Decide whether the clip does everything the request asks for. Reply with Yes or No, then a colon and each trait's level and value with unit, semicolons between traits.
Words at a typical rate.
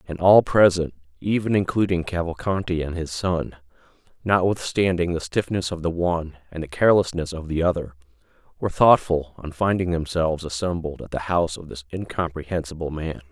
Yes: average, 155 wpm